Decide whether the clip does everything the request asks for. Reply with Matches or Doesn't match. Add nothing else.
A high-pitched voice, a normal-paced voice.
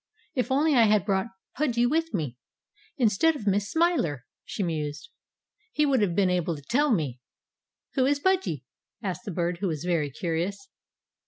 Matches